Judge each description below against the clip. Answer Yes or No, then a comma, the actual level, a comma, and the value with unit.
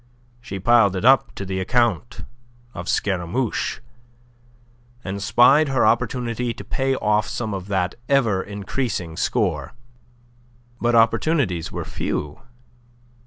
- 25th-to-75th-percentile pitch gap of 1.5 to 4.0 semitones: No, average, 4.5 semitones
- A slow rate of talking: Yes, slow, 120 wpm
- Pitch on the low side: Yes, low, 110 Hz